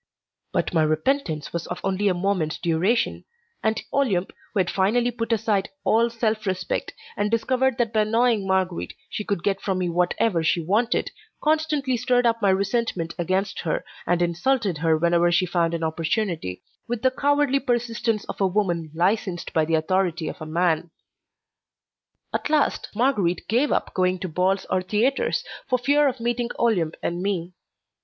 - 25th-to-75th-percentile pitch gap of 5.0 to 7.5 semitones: Yes, average, 5.3 semitones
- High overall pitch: Yes, high, 195 Hz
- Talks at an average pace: Yes, average, 170 wpm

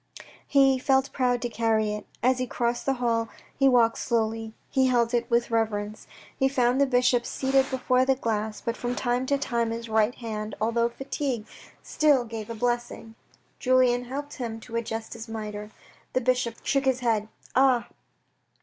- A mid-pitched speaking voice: No, high, 240 Hz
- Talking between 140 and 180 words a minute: No, average, 195 wpm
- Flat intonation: Yes, narrow, 2.3 semitones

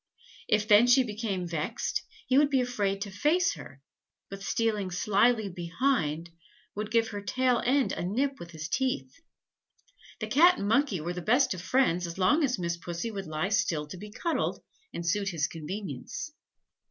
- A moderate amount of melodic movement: No, wide, 6.3 semitones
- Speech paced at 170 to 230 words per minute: Yes, average, 175 wpm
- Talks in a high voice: Yes, high, 205 Hz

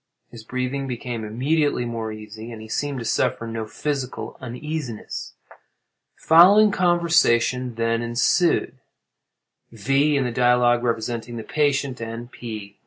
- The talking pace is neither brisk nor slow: No, slow, 125 wpm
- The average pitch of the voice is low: Yes, low, 120 Hz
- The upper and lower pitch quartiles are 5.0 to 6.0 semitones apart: No, average, 3.6 semitones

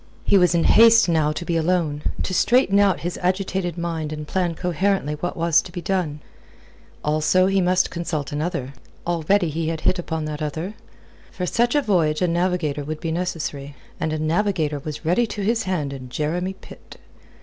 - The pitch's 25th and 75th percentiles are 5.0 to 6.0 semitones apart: No, average, 3.3 semitones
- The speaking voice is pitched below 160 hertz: No, medium, 170 Hz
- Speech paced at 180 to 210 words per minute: Yes, average, 185 wpm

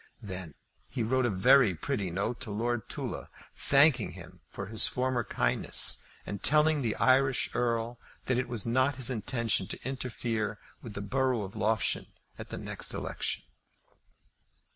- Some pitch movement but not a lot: Yes, average, 3.6 semitones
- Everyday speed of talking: Yes, average, 155 wpm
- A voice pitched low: Yes, low, 120 Hz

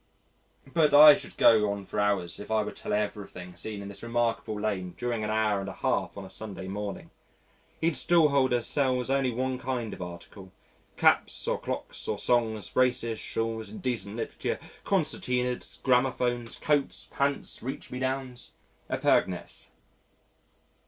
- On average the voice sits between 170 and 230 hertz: No, low, 115 Hz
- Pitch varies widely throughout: No, average, 3.8 semitones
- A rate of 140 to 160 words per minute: Yes, average, 155 wpm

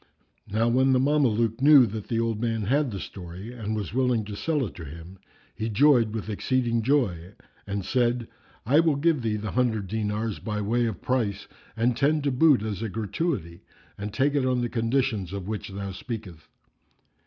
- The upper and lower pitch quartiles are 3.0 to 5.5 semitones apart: Yes, average, 4.0 semitones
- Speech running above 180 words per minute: Yes, average, 190 wpm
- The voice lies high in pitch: No, low, 115 Hz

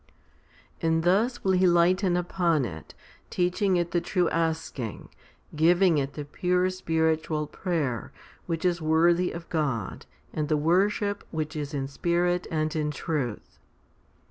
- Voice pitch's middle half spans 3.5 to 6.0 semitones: No, average, 2.8 semitones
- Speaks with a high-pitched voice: No, medium, 165 Hz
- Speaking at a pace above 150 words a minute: No, average, 145 wpm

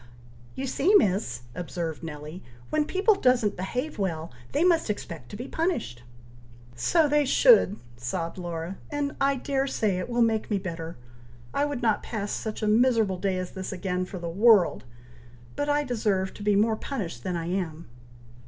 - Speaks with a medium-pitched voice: No, high, 205 Hz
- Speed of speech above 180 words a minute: No, average, 175 wpm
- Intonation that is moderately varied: No, wide, 6.9 semitones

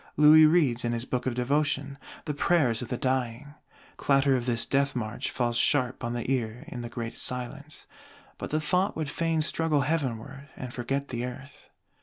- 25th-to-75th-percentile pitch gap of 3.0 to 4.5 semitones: Yes, average, 3.4 semitones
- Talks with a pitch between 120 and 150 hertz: Yes, low, 135 Hz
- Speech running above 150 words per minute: Yes, average, 185 wpm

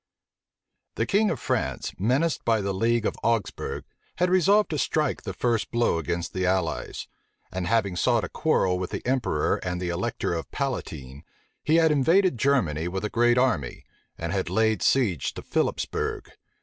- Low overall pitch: Yes, low, 115 Hz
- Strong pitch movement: Yes, wide, 6.9 semitones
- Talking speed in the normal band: Yes, average, 165 wpm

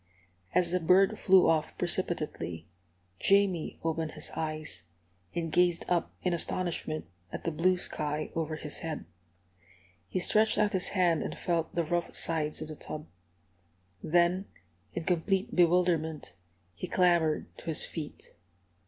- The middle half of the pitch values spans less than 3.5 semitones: Yes, narrow, 2.6 semitones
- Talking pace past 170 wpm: No, average, 140 wpm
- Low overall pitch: No, medium, 170 Hz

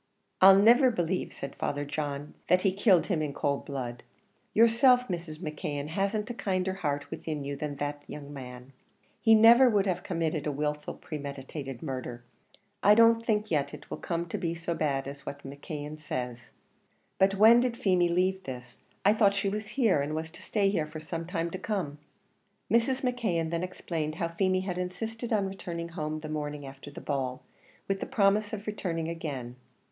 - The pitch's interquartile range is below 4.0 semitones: No, wide, 5.4 semitones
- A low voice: No, medium, 170 Hz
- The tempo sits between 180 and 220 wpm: Yes, average, 185 wpm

